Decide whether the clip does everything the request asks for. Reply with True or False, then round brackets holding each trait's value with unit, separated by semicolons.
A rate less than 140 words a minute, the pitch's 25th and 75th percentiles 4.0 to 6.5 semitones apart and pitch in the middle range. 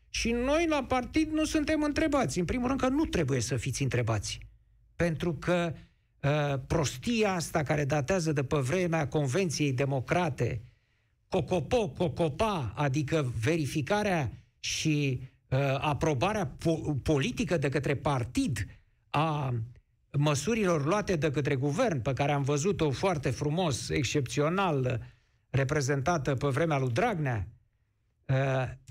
True (120 wpm; 5.0 semitones; 150 Hz)